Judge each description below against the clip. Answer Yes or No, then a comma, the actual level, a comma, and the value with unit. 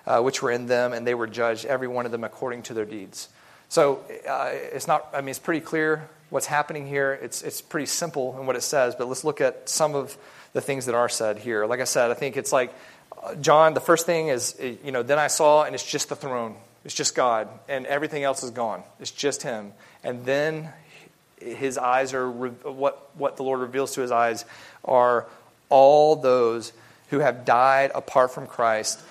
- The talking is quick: Yes, fast, 210 wpm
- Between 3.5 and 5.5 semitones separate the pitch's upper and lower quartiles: No, average, 3.1 semitones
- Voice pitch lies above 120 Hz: Yes, low, 130 Hz